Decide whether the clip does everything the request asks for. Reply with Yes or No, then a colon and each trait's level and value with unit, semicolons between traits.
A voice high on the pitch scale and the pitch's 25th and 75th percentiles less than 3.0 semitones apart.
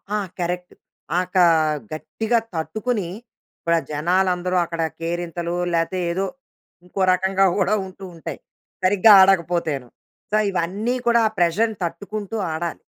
No: medium, 180 Hz; narrow, 2.6 semitones